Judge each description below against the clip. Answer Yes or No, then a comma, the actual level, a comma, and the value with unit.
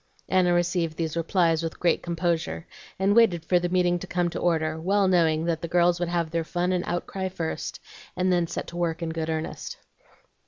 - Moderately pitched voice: Yes, medium, 175 Hz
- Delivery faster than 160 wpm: Yes, fast, 205 wpm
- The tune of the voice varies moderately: No, narrow, 1.4 semitones